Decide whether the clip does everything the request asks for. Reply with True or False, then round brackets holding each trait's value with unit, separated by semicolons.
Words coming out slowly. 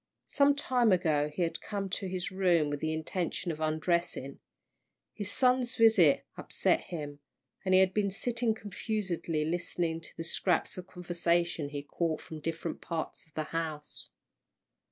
False (160 wpm)